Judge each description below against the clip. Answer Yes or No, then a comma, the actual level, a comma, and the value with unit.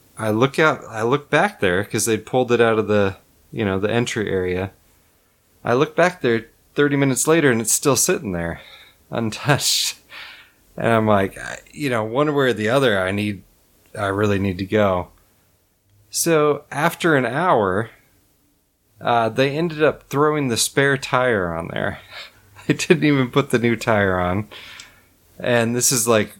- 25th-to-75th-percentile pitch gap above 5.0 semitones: Yes, wide, 5.4 semitones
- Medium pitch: No, low, 115 Hz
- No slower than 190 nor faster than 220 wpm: No, average, 175 wpm